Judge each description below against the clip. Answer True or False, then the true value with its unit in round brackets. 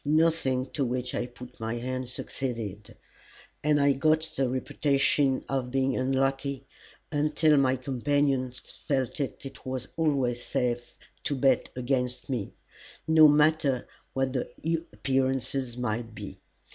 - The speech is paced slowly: True (125 wpm)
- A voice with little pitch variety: True (2.1 semitones)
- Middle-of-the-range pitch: False (130 Hz)